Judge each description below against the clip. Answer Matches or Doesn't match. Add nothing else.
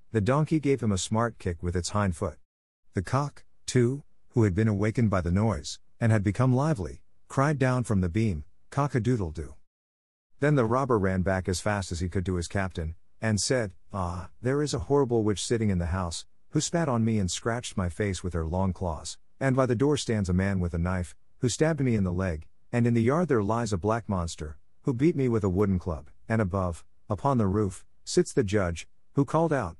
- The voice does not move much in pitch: Doesn't match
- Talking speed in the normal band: Doesn't match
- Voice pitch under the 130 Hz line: Matches